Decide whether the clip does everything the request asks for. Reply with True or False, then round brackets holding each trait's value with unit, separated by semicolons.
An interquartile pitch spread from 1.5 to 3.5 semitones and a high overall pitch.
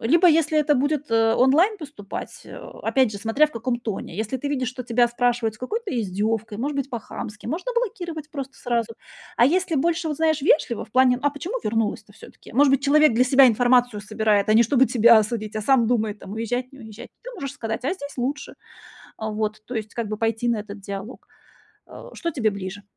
False (4.7 semitones; 245 Hz)